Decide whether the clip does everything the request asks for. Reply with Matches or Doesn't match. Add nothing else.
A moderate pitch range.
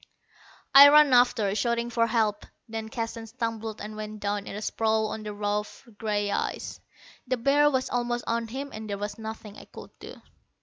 Doesn't match